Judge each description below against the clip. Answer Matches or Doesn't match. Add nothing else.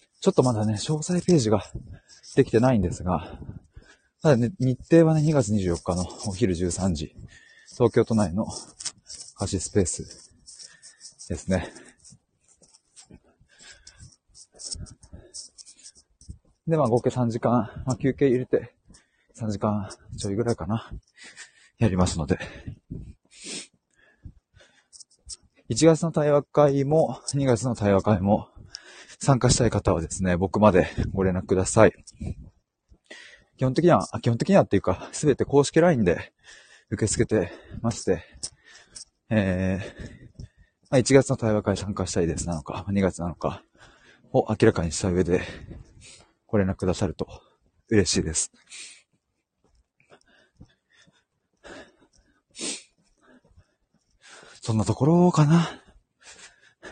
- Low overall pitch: Matches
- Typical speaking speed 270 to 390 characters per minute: Doesn't match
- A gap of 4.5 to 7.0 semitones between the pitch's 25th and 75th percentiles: Matches